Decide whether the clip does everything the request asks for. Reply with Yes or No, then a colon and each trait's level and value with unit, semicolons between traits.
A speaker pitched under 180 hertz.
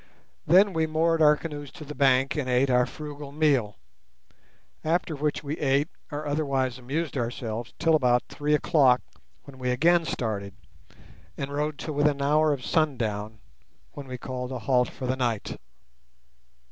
Yes: medium, 140 Hz